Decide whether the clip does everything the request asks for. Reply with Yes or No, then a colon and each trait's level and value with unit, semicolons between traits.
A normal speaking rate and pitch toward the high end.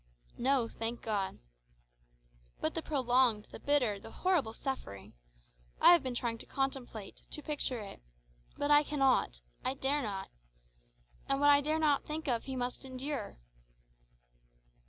Yes: average, 145 wpm; very high, 265 Hz